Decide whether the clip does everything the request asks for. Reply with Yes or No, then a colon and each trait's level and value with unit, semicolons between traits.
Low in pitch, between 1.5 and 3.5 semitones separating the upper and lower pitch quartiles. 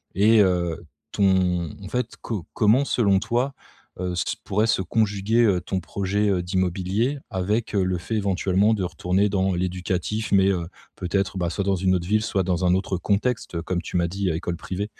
Yes: very low, 95 Hz; narrow, 2.6 semitones